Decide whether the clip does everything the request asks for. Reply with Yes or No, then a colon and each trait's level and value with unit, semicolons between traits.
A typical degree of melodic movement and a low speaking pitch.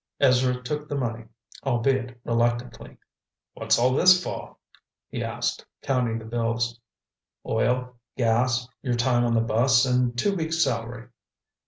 No: narrow, 1.7 semitones; low, 125 Hz